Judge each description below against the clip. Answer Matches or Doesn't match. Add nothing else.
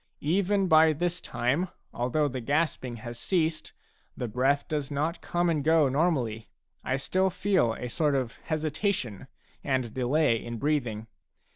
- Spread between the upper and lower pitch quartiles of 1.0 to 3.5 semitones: Doesn't match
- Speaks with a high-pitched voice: Doesn't match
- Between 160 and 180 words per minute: Doesn't match